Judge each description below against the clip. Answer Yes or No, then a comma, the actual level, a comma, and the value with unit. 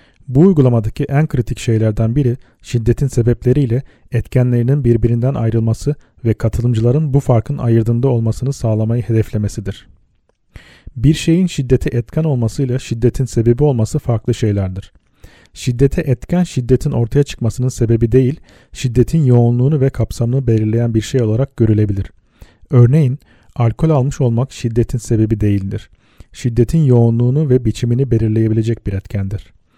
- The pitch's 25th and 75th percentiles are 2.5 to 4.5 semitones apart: Yes, average, 3.0 semitones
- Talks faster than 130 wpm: No, average, 120 wpm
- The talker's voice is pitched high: No, low, 120 Hz